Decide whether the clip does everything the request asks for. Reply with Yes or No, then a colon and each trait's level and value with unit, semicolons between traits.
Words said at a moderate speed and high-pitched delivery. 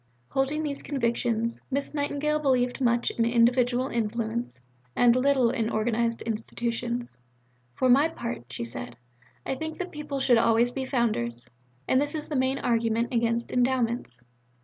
Yes: average, 150 wpm; high, 240 Hz